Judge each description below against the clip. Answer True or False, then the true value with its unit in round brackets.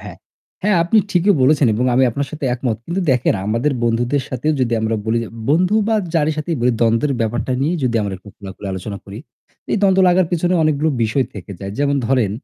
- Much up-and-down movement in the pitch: True (5.8 semitones)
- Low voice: True (130 Hz)